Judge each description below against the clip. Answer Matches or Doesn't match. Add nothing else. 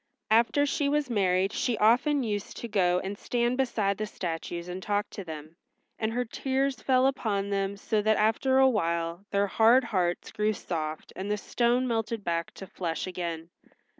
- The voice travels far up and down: Doesn't match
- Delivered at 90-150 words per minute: Doesn't match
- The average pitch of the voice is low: Doesn't match